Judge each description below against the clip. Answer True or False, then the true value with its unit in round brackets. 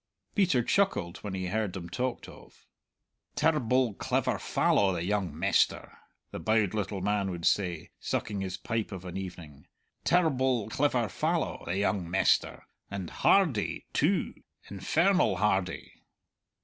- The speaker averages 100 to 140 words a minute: True (135 wpm)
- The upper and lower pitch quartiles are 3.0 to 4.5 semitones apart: False (5.2 semitones)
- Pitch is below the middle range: True (100 Hz)